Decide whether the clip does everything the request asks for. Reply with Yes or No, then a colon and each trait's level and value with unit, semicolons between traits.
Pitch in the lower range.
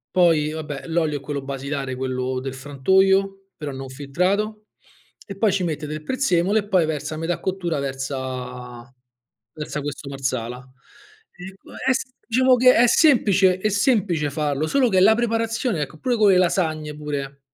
No: medium, 160 Hz